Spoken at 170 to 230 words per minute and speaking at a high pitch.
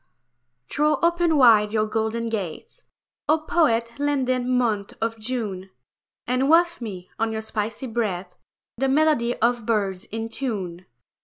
No: slow, 135 wpm; high, 230 Hz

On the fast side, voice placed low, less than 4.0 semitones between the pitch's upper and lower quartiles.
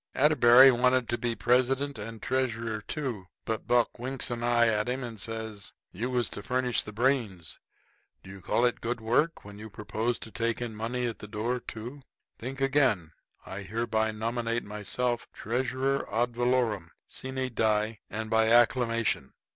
No: average, 170 wpm; low, 115 Hz; narrow, 2.4 semitones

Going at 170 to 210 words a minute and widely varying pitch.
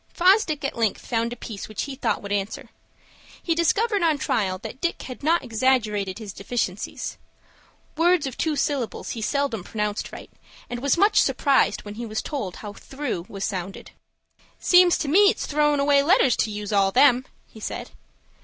Yes: average, 180 wpm; wide, 6.2 semitones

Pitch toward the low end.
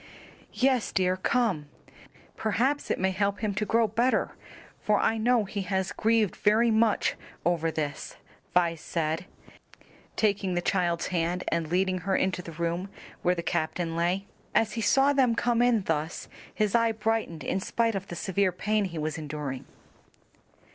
No: high, 190 Hz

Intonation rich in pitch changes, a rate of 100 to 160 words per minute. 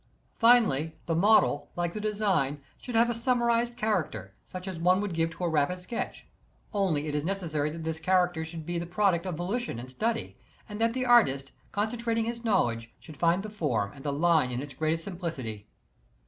No: wide, 5.9 semitones; average, 200 wpm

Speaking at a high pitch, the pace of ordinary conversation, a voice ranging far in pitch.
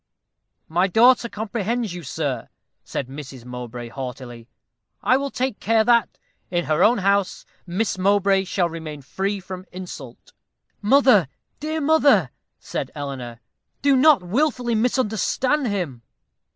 No: high, 195 Hz; slow, 125 wpm; wide, 8.2 semitones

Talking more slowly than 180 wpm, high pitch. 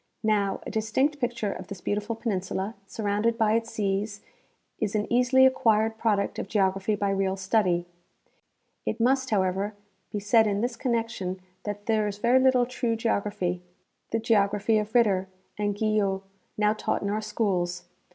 Yes: average, 160 wpm; high, 210 Hz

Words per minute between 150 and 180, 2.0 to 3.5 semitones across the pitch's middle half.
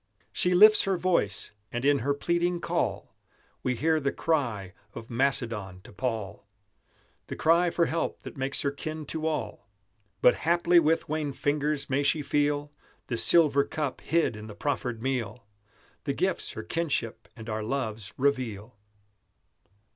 No: average, 155 wpm; wide, 5.5 semitones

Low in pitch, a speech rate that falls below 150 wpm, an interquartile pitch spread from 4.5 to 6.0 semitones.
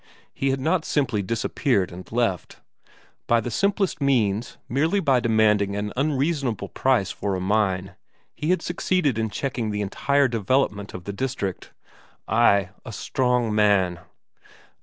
Yes: low, 115 Hz; average, 140 wpm; average, 5.2 semitones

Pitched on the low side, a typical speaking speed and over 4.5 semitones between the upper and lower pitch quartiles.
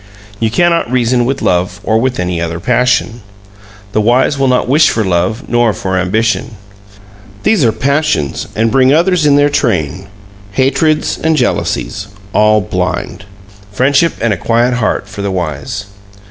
Yes: low, 115 Hz; average, 155 wpm; average, 5.2 semitones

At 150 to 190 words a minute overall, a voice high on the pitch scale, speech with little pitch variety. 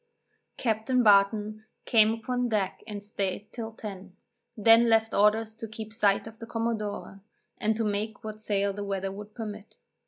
Yes: average, 160 wpm; high, 215 Hz; narrow, 1.7 semitones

